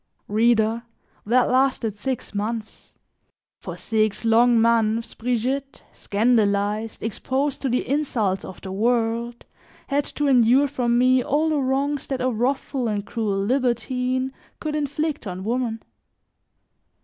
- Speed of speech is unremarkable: No, slow, 125 wpm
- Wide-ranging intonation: No, average, 3.1 semitones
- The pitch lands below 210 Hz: No, high, 240 Hz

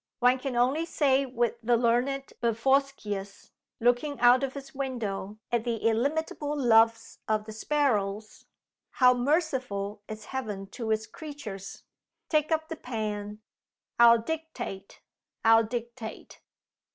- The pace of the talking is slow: Yes, slow, 125 wpm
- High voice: Yes, high, 240 Hz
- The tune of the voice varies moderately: Yes, average, 4.0 semitones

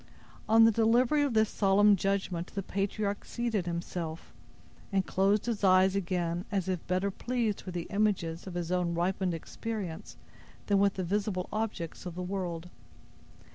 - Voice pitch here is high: Yes, high, 195 Hz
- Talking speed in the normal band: Yes, average, 160 wpm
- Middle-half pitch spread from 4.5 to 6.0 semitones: No, average, 3.0 semitones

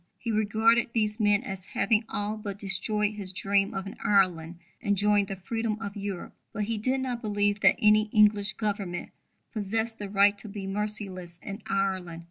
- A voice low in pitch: No, high, 205 Hz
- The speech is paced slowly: No, average, 175 wpm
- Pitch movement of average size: No, narrow, 1.6 semitones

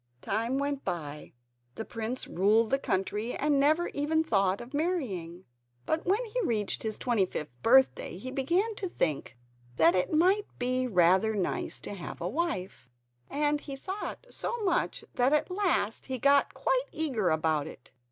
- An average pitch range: No, wide, 8.6 semitones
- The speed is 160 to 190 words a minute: Yes, average, 165 wpm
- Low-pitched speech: No, very high, 255 Hz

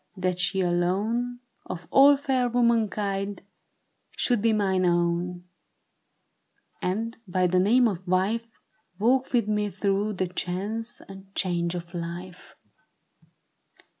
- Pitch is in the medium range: No, high, 195 Hz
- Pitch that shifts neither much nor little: Yes, average, 4.0 semitones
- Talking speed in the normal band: No, slow, 115 wpm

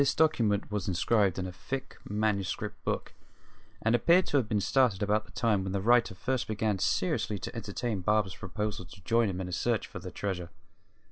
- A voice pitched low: Yes, low, 105 Hz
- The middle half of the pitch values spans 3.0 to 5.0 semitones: Yes, average, 3.5 semitones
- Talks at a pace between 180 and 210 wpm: Yes, average, 200 wpm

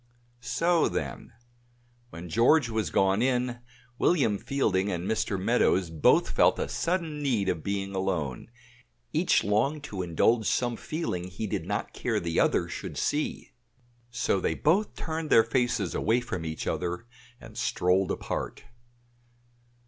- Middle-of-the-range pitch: No, low, 110 Hz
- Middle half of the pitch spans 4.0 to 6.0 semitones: Yes, wide, 5.6 semitones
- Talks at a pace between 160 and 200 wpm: No, average, 140 wpm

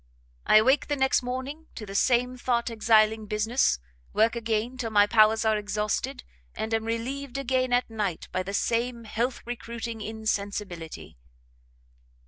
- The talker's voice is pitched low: No, high, 225 Hz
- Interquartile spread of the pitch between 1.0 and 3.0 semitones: Yes, narrow, 2.6 semitones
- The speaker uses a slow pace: No, average, 145 wpm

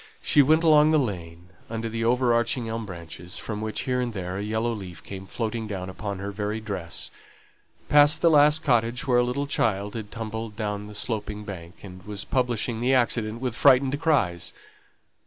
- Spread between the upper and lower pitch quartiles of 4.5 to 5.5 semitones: No, average, 3.8 semitones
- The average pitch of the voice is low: Yes, low, 110 Hz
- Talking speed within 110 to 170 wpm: No, average, 190 wpm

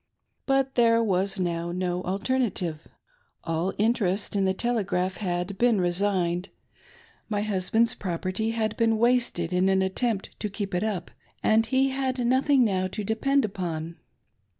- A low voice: No, high, 200 Hz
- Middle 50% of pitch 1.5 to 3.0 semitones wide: No, average, 4.1 semitones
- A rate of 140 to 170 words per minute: Yes, average, 150 wpm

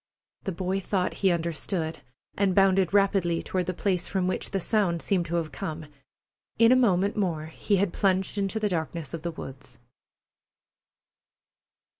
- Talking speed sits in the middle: Yes, average, 160 wpm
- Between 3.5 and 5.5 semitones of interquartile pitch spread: No, average, 2.8 semitones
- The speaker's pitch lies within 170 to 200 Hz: Yes, medium, 185 Hz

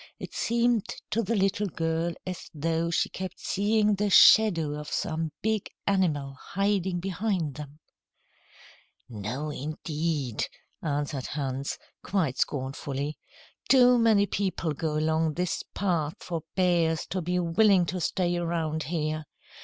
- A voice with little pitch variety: No, average, 4.3 semitones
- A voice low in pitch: No, medium, 170 Hz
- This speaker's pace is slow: Yes, slow, 130 wpm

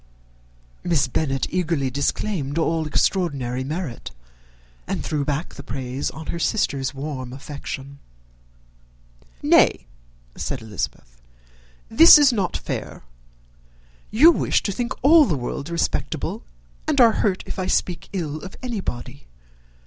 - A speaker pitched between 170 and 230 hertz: No, medium, 155 Hz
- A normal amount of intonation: No, wide, 6.0 semitones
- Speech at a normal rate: No, slow, 125 wpm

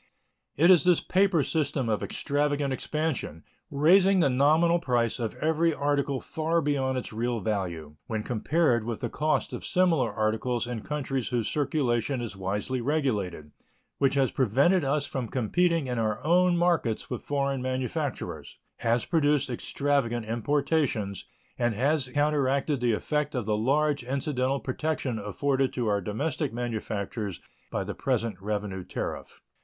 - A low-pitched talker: Yes, low, 130 Hz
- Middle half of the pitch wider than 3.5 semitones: Yes, average, 4.6 semitones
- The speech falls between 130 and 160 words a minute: Yes, average, 145 wpm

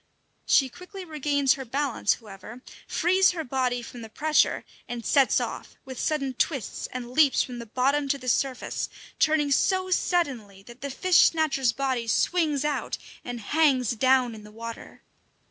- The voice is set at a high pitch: Yes, very high, 265 Hz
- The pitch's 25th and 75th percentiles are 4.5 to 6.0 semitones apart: No, average, 3.9 semitones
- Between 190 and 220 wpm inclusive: No, average, 165 wpm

